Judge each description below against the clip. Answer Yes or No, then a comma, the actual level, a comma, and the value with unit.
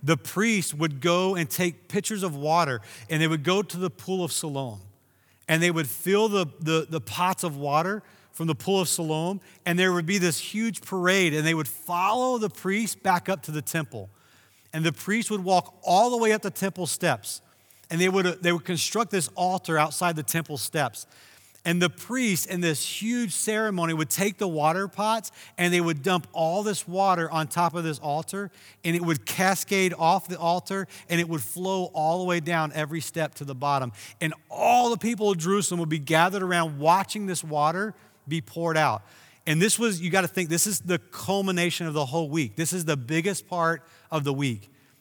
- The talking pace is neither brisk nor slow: No, fast, 210 wpm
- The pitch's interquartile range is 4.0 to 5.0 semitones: No, average, 3.4 semitones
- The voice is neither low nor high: Yes, medium, 170 Hz